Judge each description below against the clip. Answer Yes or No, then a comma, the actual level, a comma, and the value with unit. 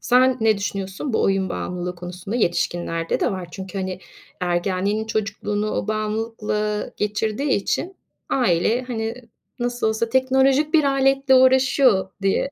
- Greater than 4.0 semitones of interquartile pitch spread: Yes, average, 5.1 semitones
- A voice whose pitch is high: Yes, high, 215 Hz